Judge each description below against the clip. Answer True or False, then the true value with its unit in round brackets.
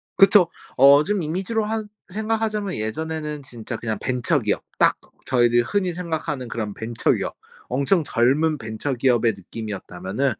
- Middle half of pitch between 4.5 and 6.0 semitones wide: False (7.4 semitones)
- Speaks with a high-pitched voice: False (140 Hz)